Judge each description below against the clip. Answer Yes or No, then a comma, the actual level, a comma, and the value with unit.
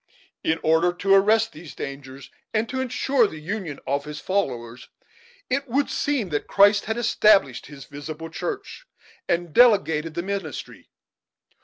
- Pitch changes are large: Yes, wide, 6.7 semitones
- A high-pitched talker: No, medium, 180 Hz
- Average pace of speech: Yes, average, 145 wpm